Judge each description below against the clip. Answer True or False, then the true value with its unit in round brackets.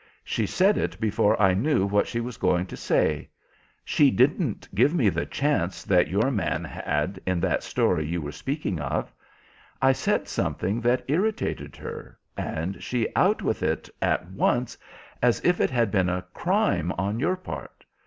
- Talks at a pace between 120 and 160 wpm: False (175 wpm)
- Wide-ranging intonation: True (6.5 semitones)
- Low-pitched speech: True (105 Hz)